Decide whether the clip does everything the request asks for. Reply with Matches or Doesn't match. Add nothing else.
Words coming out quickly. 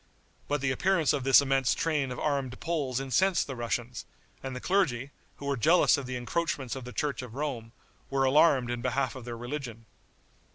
Doesn't match